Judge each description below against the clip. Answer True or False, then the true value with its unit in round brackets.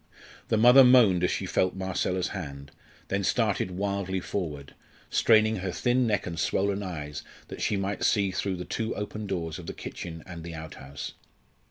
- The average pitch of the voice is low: True (95 Hz)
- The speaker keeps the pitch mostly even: False (3.3 semitones)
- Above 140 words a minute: True (175 wpm)